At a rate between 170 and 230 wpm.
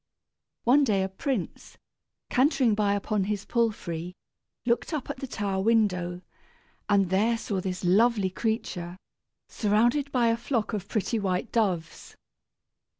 No: slow, 135 wpm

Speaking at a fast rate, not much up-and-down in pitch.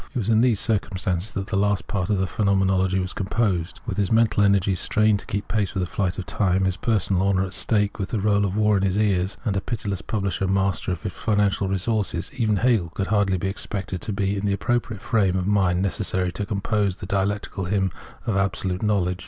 Yes: fast, 225 wpm; narrow, 1.8 semitones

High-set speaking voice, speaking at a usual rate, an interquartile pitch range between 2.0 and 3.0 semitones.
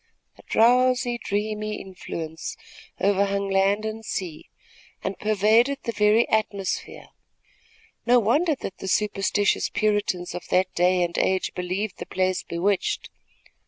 No: high, 205 Hz; slow, 125 wpm; narrow, 2.5 semitones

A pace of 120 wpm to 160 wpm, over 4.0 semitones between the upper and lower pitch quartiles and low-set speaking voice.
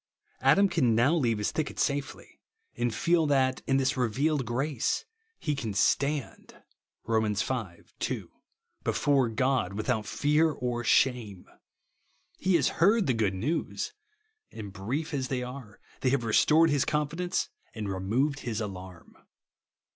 Yes: average, 140 wpm; average, 5.2 semitones; low, 130 Hz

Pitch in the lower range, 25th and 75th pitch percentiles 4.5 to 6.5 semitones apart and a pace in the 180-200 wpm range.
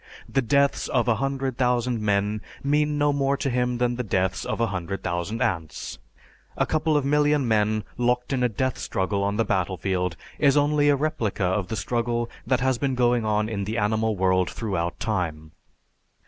Yes: low, 115 Hz; average, 5.1 semitones; average, 190 wpm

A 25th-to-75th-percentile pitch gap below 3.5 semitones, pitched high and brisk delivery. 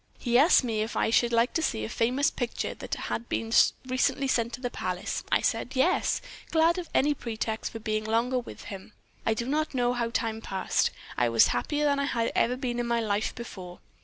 Yes: average, 3.0 semitones; high, 235 Hz; fast, 220 wpm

